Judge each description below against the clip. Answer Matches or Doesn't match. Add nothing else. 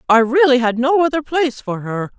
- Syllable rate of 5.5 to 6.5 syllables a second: Matches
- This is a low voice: Doesn't match